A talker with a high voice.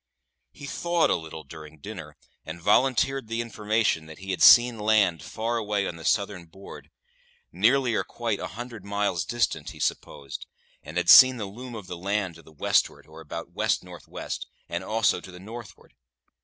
No: low, 100 Hz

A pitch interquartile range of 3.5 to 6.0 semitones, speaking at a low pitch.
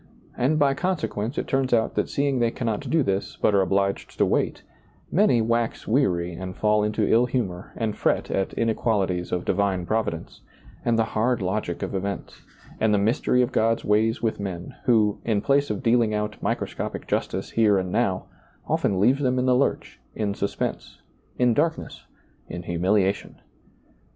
Yes: average, 3.9 semitones; low, 110 Hz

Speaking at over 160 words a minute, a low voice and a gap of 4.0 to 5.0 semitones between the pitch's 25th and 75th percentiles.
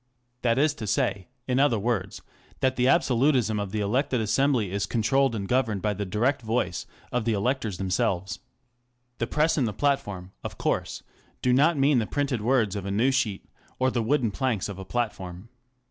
Yes: average, 190 wpm; low, 115 Hz; average, 4.7 semitones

